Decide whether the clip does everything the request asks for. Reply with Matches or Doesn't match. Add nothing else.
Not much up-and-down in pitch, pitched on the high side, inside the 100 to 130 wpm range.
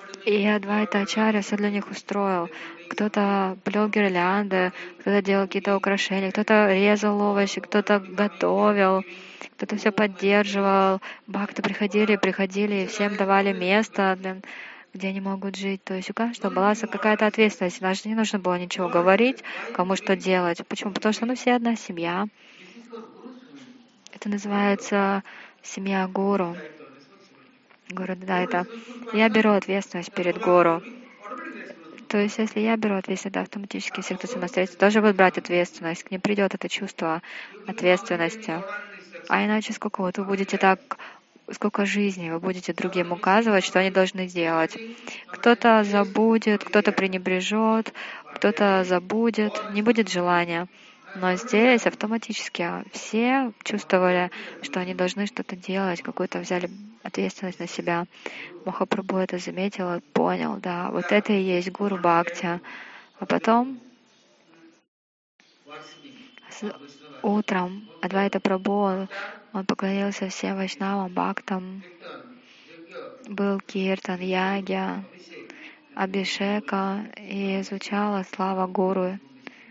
Matches